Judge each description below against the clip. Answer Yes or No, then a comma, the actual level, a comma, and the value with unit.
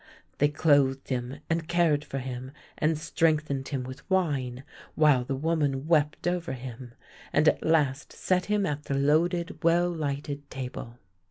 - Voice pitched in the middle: Yes, medium, 145 Hz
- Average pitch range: Yes, average, 3.6 semitones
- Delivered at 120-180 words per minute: Yes, average, 155 wpm